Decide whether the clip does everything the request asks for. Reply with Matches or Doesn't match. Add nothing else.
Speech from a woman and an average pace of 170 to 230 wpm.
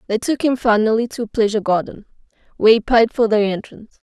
Matches